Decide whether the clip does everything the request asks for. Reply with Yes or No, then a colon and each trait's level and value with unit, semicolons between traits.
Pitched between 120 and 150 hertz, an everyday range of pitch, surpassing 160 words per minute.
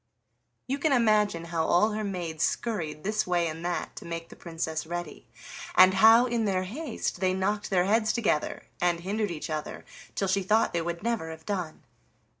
No: medium, 185 Hz; average, 4.3 semitones; average, 195 wpm